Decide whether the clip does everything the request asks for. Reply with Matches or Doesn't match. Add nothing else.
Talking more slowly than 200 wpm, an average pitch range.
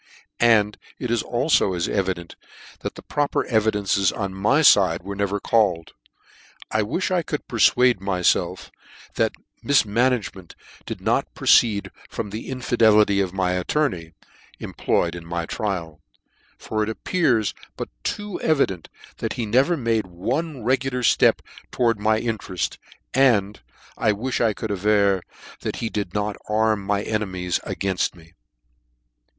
Matches